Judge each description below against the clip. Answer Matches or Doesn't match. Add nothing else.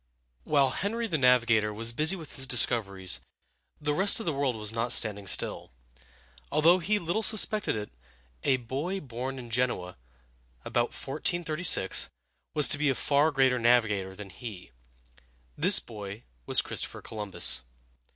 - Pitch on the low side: Matches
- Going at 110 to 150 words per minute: Matches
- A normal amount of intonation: Doesn't match